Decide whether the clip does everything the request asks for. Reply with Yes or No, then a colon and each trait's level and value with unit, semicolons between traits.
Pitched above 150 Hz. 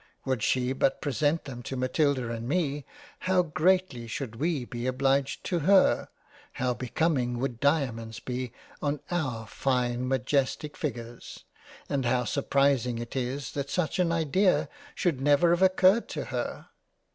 No: low, 135 Hz